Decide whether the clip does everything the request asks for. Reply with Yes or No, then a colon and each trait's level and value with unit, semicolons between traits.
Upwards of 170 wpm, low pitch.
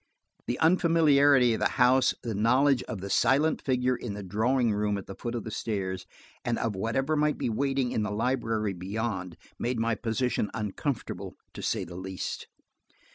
Yes: average, 180 wpm; low, 115 Hz